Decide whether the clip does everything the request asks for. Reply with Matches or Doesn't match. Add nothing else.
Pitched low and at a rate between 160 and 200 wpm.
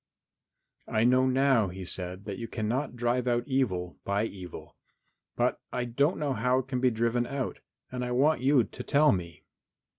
Matches